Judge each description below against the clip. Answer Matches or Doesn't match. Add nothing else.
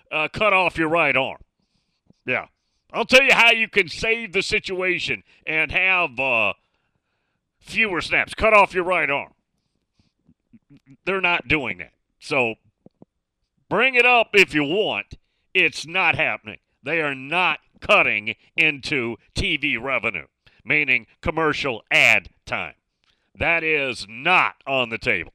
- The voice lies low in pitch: Doesn't match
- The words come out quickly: Doesn't match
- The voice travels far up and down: Matches